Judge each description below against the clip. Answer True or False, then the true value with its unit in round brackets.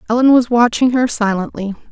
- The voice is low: False (230 Hz)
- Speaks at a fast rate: False (155 wpm)